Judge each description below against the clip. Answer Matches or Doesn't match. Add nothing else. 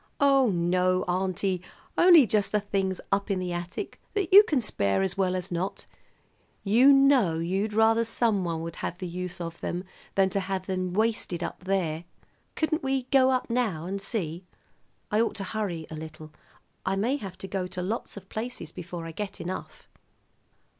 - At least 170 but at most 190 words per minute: Matches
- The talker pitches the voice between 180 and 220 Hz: Matches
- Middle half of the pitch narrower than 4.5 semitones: Matches